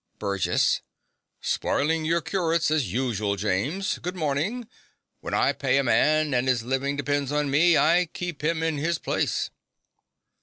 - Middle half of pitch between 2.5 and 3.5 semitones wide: No, average, 4.2 semitones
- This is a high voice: No, medium, 150 Hz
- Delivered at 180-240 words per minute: No, average, 150 wpm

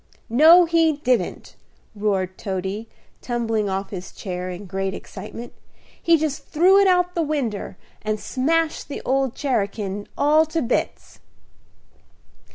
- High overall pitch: Yes, high, 240 Hz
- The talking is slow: Yes, slow, 130 wpm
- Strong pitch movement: Yes, wide, 7.8 semitones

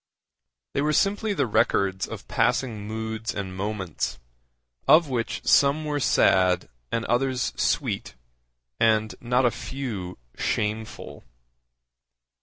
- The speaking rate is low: Yes, slow, 110 wpm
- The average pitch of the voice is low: Yes, low, 115 Hz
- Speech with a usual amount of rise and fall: Yes, average, 4.4 semitones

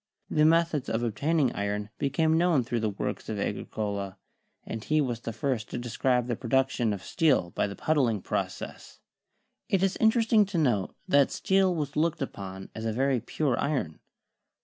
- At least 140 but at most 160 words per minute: No, average, 190 wpm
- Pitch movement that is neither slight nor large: No, wide, 6.1 semitones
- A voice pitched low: Yes, low, 130 Hz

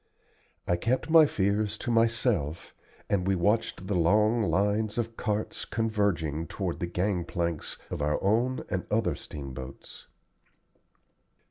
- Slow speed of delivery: Yes, slow, 130 wpm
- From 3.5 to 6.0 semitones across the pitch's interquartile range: Yes, average, 4.5 semitones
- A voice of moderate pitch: No, low, 100 Hz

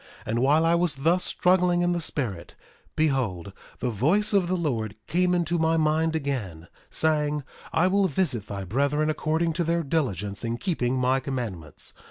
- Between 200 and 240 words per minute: No, average, 175 wpm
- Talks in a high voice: No, medium, 150 Hz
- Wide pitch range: Yes, wide, 5.9 semitones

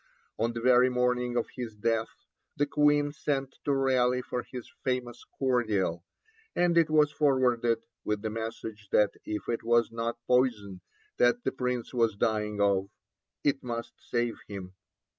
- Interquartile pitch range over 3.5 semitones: No, narrow, 2.5 semitones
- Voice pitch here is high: No, low, 120 Hz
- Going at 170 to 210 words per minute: No, average, 155 wpm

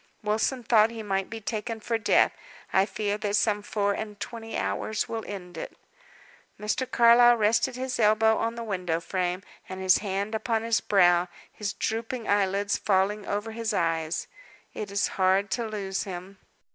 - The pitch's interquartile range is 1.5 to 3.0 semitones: Yes, average, 2.7 semitones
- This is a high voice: Yes, high, 210 Hz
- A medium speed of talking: Yes, average, 170 wpm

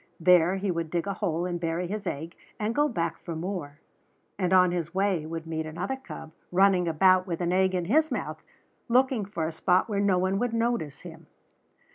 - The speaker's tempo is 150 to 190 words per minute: No, fast, 205 wpm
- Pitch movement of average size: Yes, average, 3.2 semitones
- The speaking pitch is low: No, medium, 180 Hz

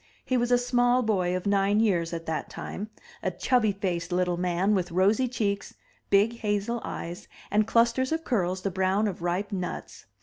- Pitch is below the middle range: No, high, 200 Hz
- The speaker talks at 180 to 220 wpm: Yes, average, 190 wpm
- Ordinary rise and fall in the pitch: Yes, average, 4.3 semitones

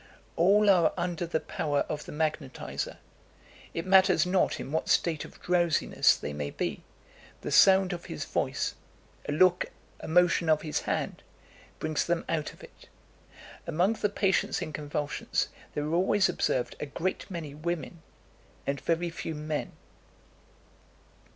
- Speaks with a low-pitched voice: No, medium, 165 Hz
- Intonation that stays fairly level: No, average, 3.0 semitones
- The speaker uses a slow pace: No, average, 150 wpm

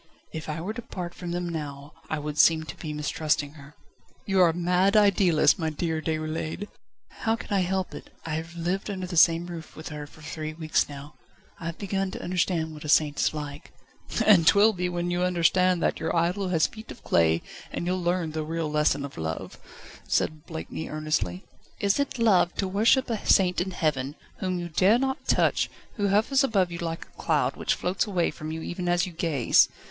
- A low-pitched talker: No, medium, 170 Hz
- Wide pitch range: No, average, 3.1 semitones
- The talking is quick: Yes, fast, 210 wpm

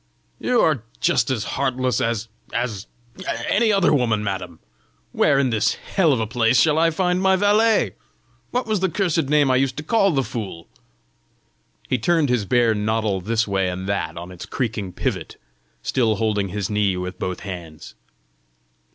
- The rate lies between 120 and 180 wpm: Yes, average, 170 wpm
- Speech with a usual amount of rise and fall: No, wide, 7.3 semitones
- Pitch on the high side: No, low, 115 Hz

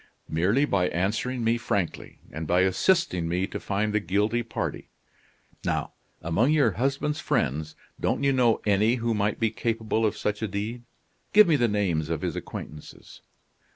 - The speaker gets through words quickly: No, average, 165 wpm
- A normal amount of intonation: Yes, average, 4.3 semitones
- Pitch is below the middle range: Yes, low, 105 Hz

